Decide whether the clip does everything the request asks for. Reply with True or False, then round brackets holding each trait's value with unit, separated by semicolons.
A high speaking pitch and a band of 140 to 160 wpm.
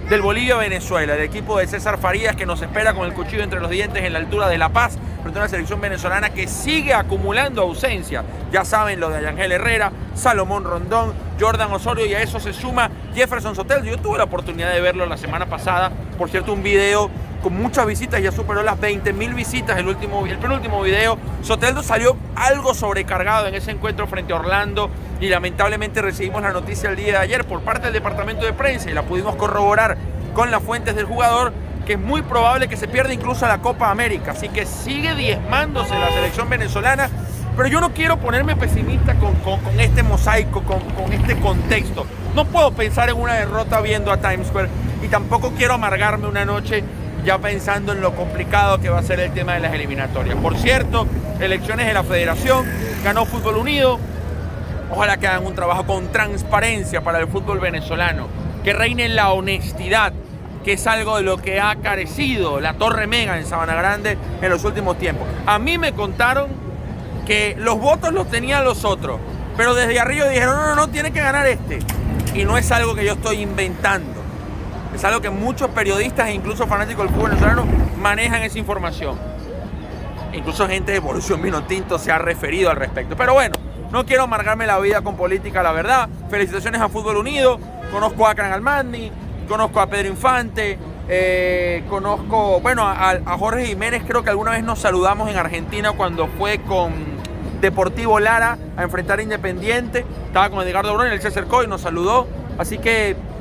False (200 Hz; 190 wpm)